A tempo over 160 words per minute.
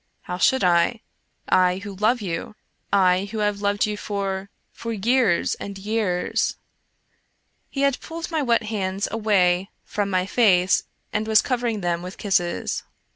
Yes: average, 170 wpm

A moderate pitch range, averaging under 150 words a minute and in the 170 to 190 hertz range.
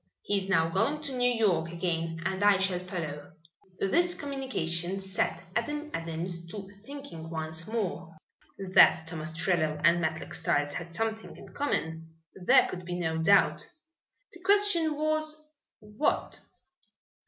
No: wide, 7.1 semitones; average, 140 wpm; medium, 185 Hz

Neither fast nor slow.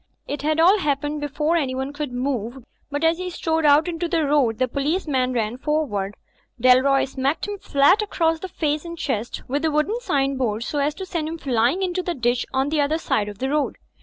No: fast, 215 wpm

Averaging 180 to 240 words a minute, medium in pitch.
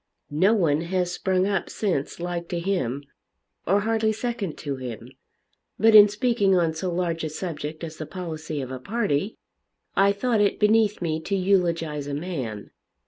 No: average, 170 wpm; medium, 180 Hz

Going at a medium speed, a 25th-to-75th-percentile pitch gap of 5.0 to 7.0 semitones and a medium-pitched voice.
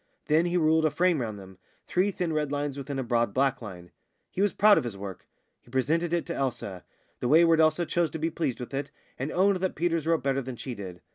No: fast, 240 wpm; wide, 5.4 semitones; medium, 145 Hz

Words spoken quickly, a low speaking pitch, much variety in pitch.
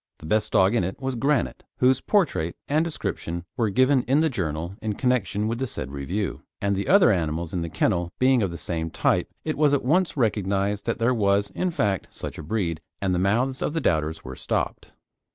Yes: fast, 215 wpm; low, 105 Hz; wide, 6.9 semitones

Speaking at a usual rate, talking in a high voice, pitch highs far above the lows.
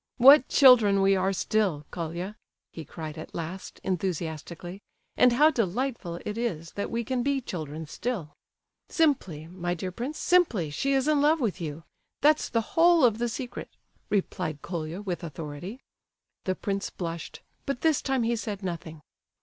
Yes: average, 150 wpm; high, 195 Hz; wide, 6.9 semitones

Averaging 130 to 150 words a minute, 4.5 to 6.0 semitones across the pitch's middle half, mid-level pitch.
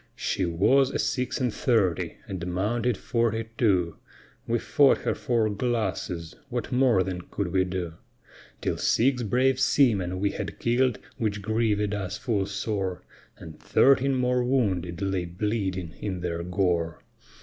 No: average, 145 wpm; average, 4.9 semitones; low, 105 Hz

